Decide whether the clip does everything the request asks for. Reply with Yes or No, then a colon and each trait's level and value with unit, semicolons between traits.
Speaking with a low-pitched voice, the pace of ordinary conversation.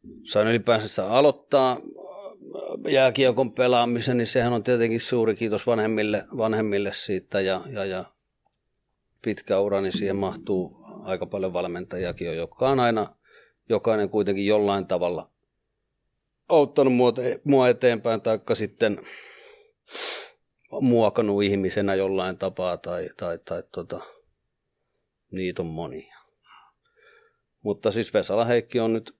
Yes: low, 115 Hz; average, 110 wpm